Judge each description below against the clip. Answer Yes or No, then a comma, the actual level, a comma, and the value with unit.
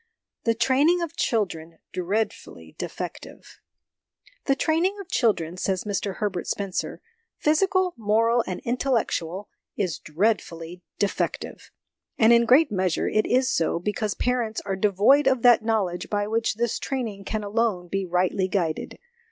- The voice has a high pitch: Yes, high, 215 Hz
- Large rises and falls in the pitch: No, average, 4.6 semitones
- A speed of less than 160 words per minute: Yes, average, 140 wpm